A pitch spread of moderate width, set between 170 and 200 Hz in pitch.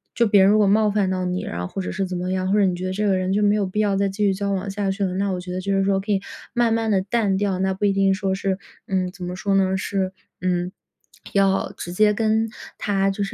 No: narrow, 1.6 semitones; high, 195 Hz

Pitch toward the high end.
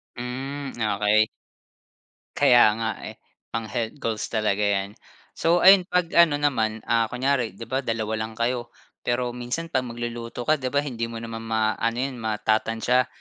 No: low, 120 Hz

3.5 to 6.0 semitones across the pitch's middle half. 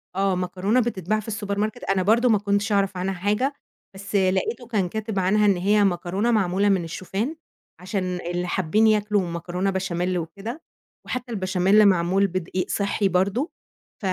No: narrow, 2.5 semitones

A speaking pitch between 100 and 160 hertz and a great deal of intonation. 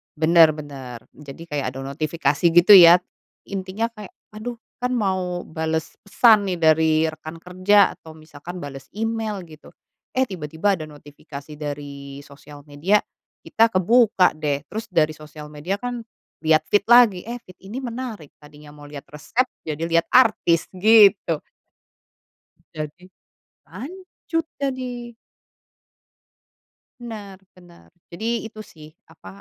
No: medium, 175 Hz; wide, 6.1 semitones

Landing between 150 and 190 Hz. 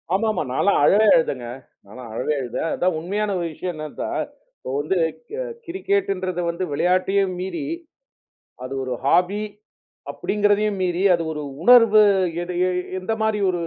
Yes: medium, 185 Hz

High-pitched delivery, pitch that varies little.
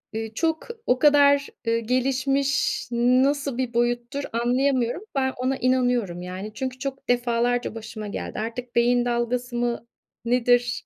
Yes: high, 245 Hz; narrow, 1.9 semitones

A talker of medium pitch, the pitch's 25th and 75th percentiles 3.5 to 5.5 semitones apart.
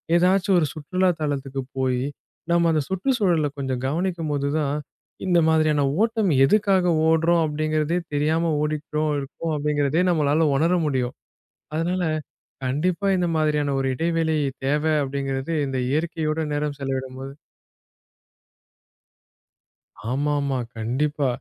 No: medium, 155 Hz; average, 3.1 semitones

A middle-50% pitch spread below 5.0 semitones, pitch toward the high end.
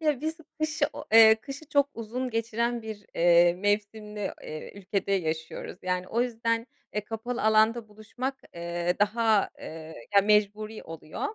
Yes: average, 3.3 semitones; high, 215 Hz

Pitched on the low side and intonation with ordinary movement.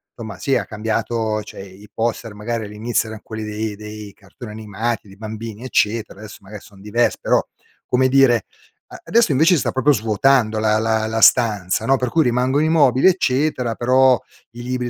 Yes: low, 115 Hz; average, 3.0 semitones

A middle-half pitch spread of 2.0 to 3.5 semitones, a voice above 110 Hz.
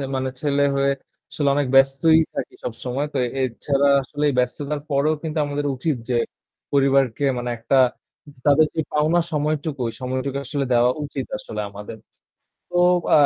Yes: narrow, 2.5 semitones; medium, 140 Hz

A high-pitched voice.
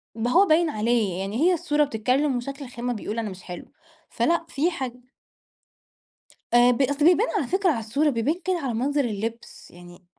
Yes: very high, 250 Hz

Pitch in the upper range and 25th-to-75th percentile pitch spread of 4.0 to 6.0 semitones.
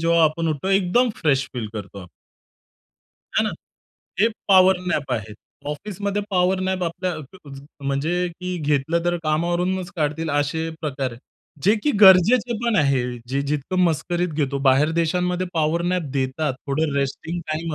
No: medium, 165 Hz; average, 4.3 semitones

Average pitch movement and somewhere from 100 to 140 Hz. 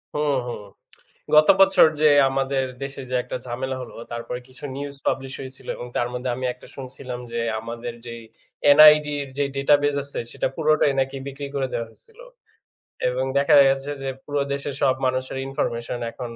No: narrow, 2.3 semitones; low, 135 Hz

